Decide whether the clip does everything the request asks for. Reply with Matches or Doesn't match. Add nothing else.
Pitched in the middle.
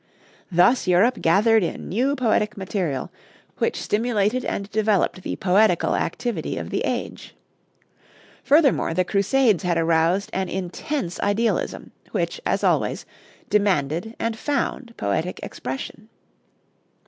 Doesn't match